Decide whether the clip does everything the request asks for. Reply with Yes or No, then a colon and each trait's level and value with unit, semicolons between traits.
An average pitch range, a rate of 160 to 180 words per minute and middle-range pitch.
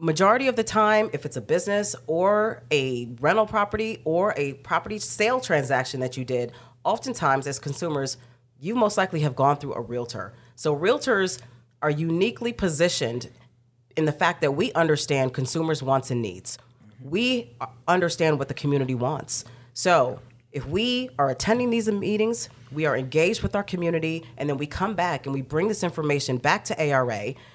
No: wide, 6.8 semitones; average, 170 wpm; medium, 150 Hz